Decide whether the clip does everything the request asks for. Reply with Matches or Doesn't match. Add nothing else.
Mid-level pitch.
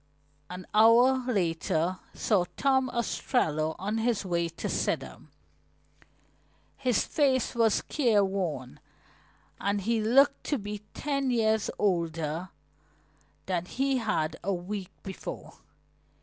Doesn't match